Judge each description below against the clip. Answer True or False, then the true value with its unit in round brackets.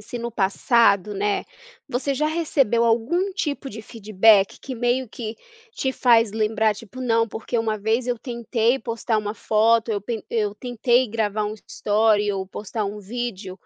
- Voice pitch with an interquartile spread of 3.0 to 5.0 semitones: False (2.6 semitones)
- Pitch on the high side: True (225 Hz)